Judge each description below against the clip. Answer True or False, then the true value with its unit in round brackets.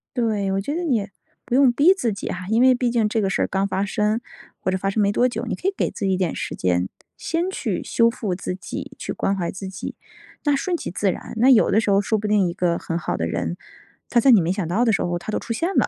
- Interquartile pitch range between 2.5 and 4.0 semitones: False (4.4 semitones)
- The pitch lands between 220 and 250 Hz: False (210 Hz)